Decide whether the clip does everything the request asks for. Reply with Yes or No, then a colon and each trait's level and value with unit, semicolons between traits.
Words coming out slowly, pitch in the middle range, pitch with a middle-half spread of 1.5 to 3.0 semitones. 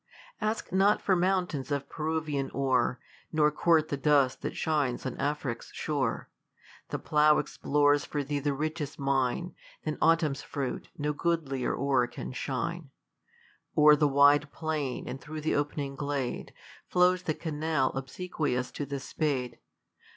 No: average, 145 wpm; medium, 145 Hz; narrow, 2.5 semitones